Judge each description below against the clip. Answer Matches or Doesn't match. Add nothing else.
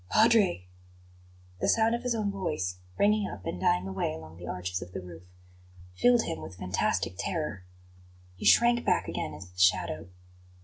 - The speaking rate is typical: Matches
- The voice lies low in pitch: Matches